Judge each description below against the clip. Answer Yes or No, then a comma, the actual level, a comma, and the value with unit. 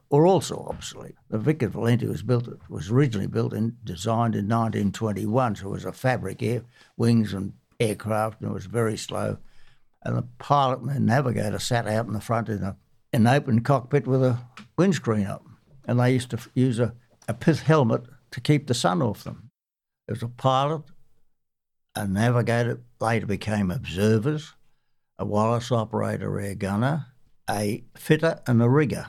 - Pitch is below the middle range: Yes, low, 115 Hz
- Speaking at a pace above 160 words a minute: Yes, average, 175 wpm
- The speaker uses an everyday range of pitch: Yes, average, 3.3 semitones